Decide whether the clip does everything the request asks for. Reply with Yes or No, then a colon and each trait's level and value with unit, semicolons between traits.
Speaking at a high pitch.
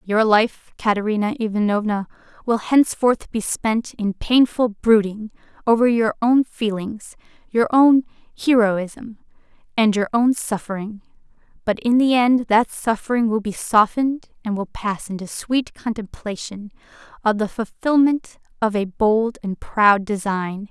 Yes: high, 220 Hz